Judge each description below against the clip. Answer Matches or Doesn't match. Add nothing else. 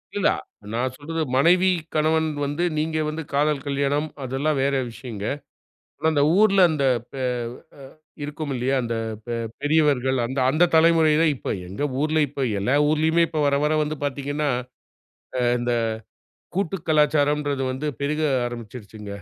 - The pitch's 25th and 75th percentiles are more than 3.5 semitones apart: Doesn't match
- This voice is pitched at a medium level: Matches